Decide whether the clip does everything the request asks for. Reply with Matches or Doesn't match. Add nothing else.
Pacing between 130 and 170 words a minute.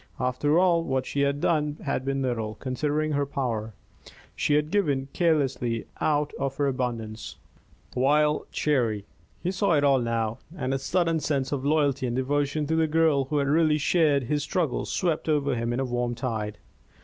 Doesn't match